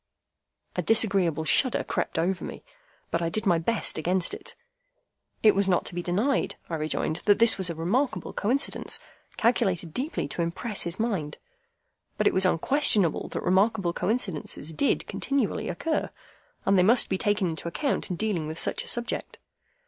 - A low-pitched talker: No, high, 190 Hz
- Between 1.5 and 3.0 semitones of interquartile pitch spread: No, average, 5.0 semitones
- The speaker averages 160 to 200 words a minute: Yes, average, 170 wpm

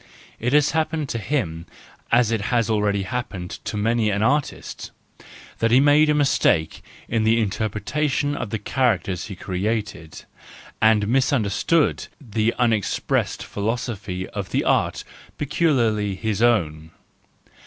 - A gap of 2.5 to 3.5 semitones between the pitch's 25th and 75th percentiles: No, average, 4.2 semitones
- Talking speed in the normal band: No, slow, 130 wpm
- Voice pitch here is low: Yes, low, 110 Hz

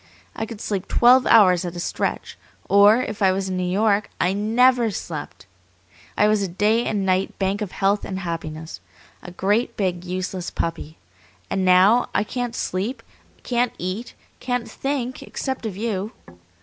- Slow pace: No, average, 165 wpm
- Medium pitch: No, high, 200 Hz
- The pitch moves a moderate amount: Yes, average, 3.7 semitones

